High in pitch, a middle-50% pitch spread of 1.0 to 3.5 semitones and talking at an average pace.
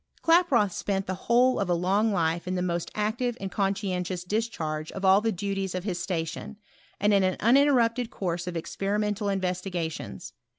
Yes: high, 195 Hz; average, 3.1 semitones; average, 170 wpm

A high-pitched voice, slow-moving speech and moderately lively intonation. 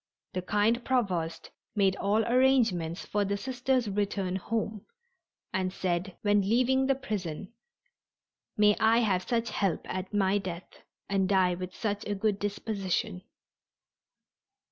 Yes: high, 205 Hz; slow, 130 wpm; average, 3.1 semitones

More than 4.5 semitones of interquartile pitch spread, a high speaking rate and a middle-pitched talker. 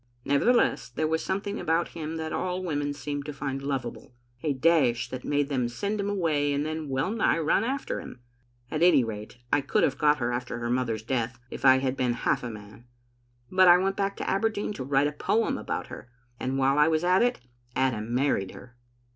Yes: average, 5.0 semitones; fast, 215 wpm; medium, 145 Hz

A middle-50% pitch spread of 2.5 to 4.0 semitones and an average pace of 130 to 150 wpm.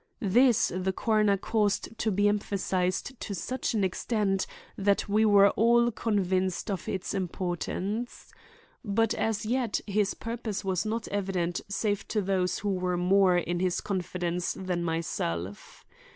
Yes: average, 2.8 semitones; average, 140 wpm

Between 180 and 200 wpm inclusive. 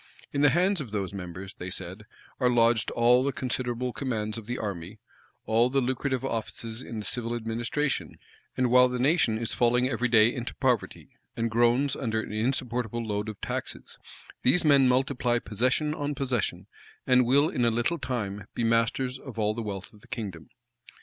Yes: average, 185 wpm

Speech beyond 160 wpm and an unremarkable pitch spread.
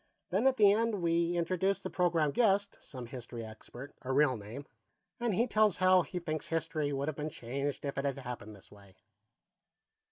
No: average, 190 wpm; wide, 6.1 semitones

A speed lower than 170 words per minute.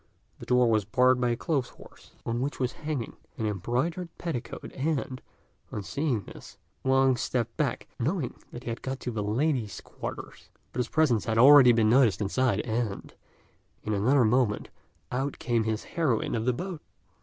No: average, 175 wpm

